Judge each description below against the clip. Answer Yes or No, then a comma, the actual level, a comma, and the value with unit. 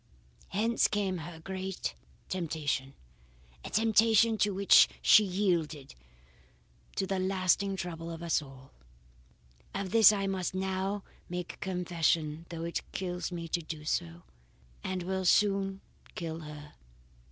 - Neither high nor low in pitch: Yes, medium, 180 Hz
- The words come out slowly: Yes, slow, 130 wpm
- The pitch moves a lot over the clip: No, average, 2.9 semitones